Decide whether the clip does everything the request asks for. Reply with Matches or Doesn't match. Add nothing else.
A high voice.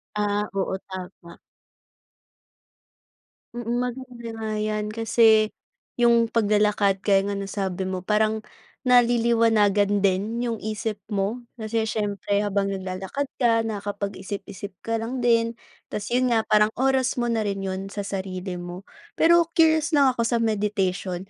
Matches